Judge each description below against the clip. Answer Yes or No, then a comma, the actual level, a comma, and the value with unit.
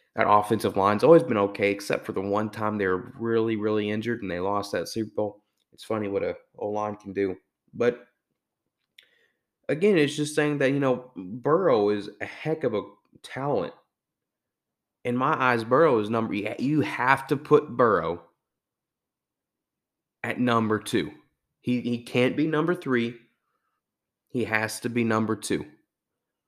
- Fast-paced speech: No, average, 160 wpm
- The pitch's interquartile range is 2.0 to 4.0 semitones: Yes, average, 3.6 semitones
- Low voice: Yes, low, 115 Hz